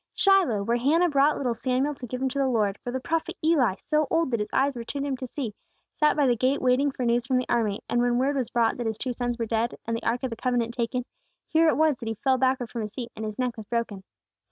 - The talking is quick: Yes, fast, 290 wpm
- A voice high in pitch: Yes, very high, 250 Hz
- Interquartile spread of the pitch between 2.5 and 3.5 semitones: Yes, average, 3.0 semitones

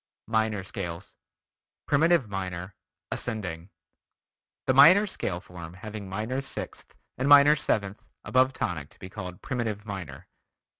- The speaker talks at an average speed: No, slow, 120 wpm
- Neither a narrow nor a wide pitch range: No, wide, 5.9 semitones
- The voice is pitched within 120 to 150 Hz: No, low, 105 Hz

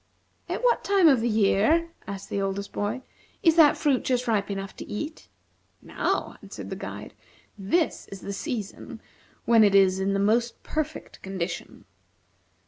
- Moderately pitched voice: No, high, 215 Hz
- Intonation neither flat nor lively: No, wide, 6.8 semitones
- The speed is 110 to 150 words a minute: No, average, 160 wpm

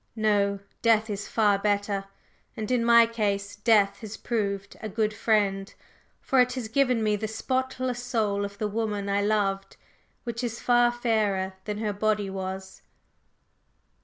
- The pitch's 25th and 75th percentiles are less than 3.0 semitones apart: Yes, narrow, 2.4 semitones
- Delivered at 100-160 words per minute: Yes, average, 155 wpm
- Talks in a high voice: Yes, high, 215 Hz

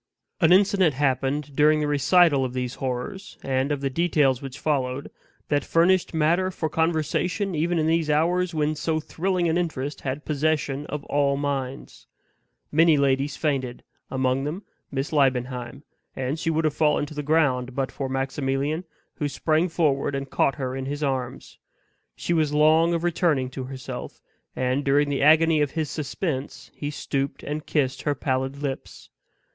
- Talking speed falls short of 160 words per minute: No, average, 165 wpm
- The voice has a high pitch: No, medium, 145 Hz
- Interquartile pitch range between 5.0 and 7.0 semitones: No, average, 3.0 semitones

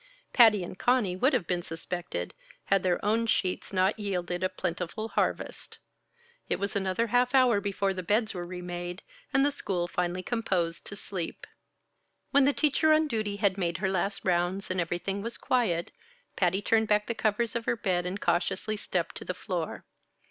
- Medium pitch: No, high, 195 Hz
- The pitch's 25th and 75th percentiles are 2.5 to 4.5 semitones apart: Yes, average, 3.9 semitones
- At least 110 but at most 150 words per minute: No, average, 180 wpm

